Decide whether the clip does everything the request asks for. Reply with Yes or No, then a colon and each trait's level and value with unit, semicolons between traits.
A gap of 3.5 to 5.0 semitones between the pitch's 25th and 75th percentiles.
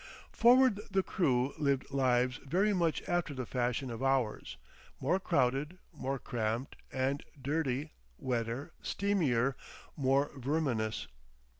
Yes: average, 4.5 semitones